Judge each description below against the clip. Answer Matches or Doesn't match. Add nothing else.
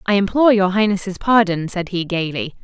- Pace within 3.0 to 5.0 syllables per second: Doesn't match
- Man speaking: Doesn't match